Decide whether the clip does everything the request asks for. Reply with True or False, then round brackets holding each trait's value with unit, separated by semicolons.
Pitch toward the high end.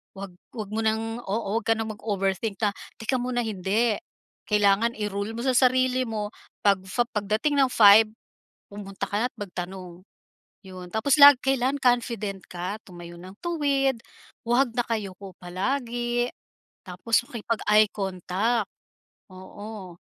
True (215 Hz)